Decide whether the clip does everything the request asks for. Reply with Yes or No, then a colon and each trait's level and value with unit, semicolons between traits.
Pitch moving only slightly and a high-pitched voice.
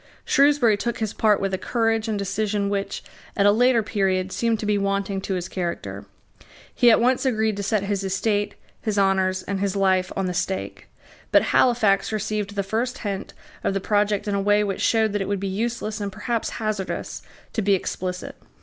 Yes: narrow, 2.0 semitones; high, 205 Hz